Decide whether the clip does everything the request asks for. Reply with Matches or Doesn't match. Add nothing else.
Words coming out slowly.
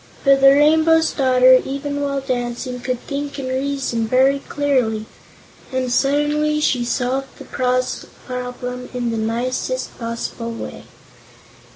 Matches